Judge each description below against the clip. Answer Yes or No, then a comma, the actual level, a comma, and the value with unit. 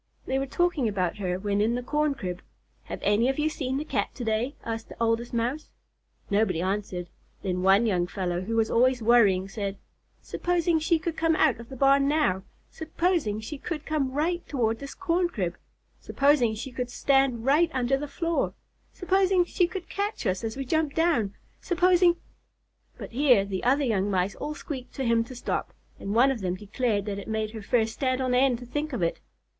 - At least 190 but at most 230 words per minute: Yes, fast, 205 wpm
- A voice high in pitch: Yes, very high, 250 Hz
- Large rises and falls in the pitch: Yes, wide, 6.3 semitones